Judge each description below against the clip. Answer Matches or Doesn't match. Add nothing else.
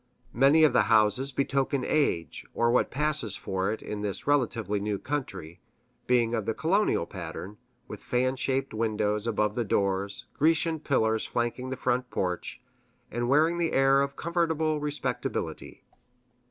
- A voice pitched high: Doesn't match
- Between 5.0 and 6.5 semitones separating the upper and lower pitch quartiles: Matches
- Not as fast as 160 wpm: Matches